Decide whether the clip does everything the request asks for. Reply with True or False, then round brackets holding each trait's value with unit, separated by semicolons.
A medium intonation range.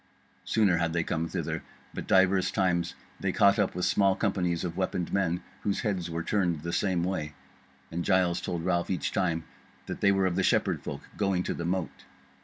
False (2.1 semitones)